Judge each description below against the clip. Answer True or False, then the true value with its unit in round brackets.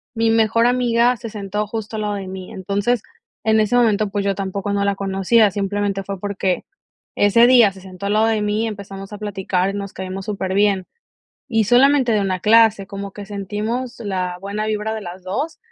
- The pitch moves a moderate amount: False (2.2 semitones)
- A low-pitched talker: False (205 Hz)